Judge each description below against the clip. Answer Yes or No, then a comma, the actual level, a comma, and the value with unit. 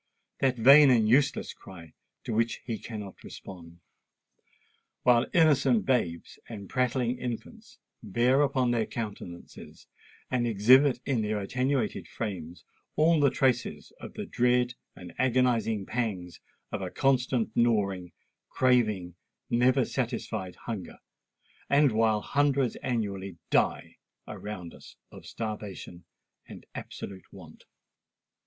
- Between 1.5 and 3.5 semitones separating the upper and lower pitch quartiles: No, average, 4.4 semitones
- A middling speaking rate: No, slow, 110 wpm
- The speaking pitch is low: Yes, low, 115 Hz